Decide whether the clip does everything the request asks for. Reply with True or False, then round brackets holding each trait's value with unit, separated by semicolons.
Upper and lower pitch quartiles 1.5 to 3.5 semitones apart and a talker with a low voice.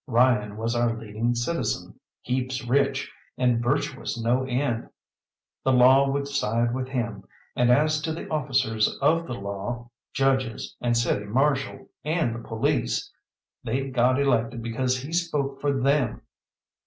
True (2.8 semitones; 125 Hz)